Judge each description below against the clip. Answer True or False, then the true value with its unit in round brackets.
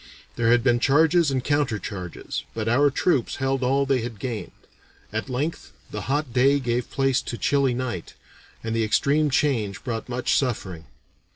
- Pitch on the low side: True (125 Hz)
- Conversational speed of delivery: True (170 wpm)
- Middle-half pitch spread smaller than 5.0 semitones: True (3.4 semitones)